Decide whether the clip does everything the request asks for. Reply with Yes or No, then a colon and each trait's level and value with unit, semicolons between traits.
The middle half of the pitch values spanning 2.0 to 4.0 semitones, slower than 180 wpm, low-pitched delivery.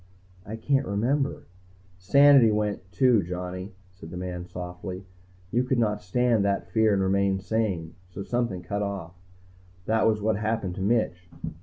Yes: average, 3.5 semitones; average, 160 wpm; low, 100 Hz